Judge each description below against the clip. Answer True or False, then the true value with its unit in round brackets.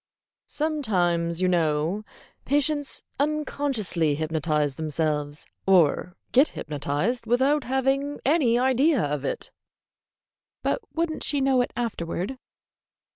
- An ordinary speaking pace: False (105 wpm)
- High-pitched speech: True (220 Hz)